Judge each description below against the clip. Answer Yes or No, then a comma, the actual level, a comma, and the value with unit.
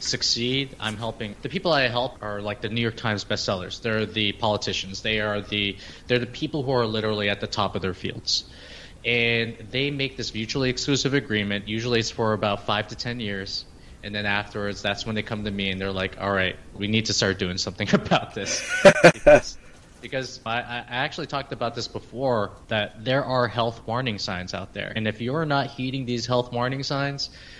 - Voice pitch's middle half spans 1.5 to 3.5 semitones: Yes, average, 3.2 semitones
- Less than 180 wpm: No, fast, 205 wpm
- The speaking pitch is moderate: No, low, 110 Hz